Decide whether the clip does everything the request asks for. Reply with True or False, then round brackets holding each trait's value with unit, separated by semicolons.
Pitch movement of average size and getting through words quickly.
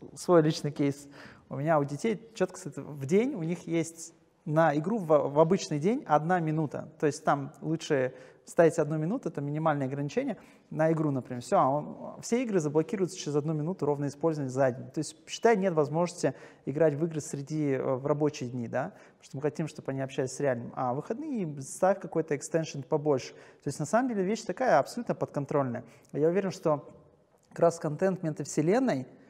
True (3.2 semitones; 180 wpm)